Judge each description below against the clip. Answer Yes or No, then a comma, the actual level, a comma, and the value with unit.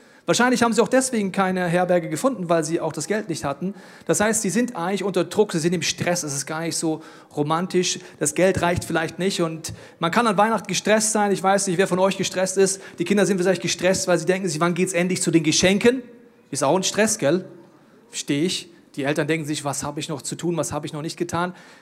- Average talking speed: No, fast, 250 wpm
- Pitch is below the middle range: No, medium, 180 Hz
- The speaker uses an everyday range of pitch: Yes, average, 3.1 semitones